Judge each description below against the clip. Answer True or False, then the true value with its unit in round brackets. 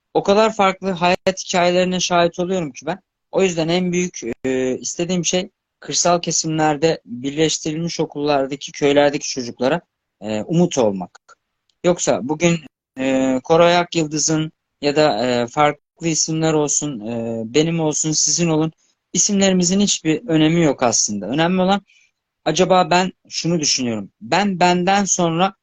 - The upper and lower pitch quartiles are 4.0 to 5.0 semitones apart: False (3.6 semitones)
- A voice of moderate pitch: True (160 Hz)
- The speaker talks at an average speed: True (130 wpm)